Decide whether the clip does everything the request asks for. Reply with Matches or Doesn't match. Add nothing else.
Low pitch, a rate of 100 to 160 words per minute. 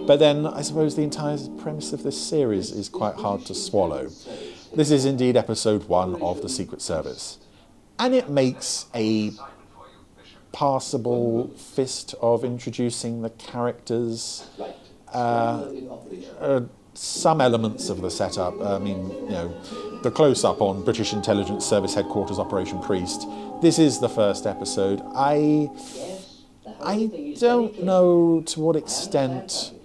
Matches